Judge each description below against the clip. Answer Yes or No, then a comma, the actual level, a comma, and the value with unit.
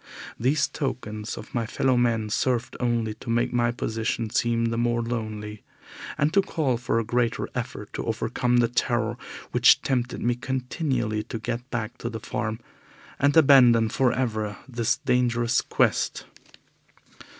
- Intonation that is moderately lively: No, narrow, 1.9 semitones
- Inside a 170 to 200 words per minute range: No, average, 155 wpm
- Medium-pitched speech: No, low, 120 Hz